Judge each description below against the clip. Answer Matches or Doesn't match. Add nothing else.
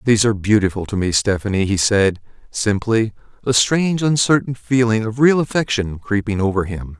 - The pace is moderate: Matches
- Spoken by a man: Matches